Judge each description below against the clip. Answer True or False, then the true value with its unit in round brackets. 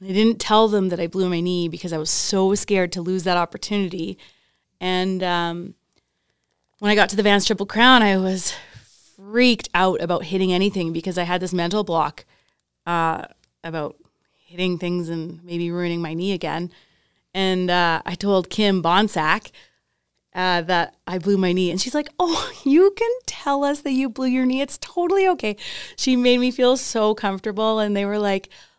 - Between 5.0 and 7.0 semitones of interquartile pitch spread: False (3.8 semitones)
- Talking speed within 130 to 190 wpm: True (185 wpm)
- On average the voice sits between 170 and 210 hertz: True (190 Hz)